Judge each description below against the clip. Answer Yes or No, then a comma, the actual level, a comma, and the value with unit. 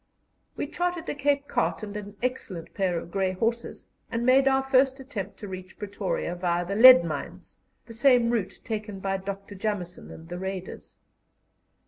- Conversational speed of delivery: Yes, average, 170 wpm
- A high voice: Yes, high, 205 Hz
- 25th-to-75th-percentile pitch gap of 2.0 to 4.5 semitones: No, average, 5.3 semitones